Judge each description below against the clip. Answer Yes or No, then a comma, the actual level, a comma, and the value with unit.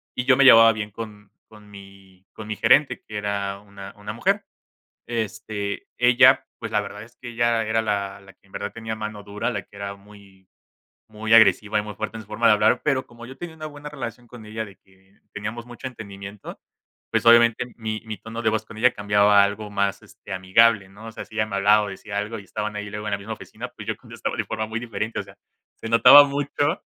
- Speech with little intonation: Yes, narrow, 2.3 semitones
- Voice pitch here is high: No, low, 110 Hz